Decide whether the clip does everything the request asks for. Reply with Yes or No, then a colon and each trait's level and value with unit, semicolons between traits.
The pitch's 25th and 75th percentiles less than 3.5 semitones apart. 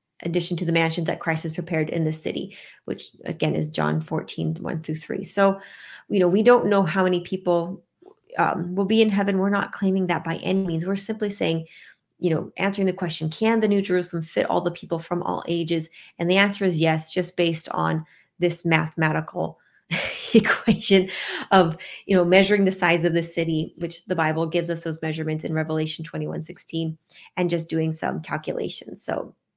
Yes: average, 3.0 semitones